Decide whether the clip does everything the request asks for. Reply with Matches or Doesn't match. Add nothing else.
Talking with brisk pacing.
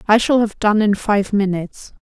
Matches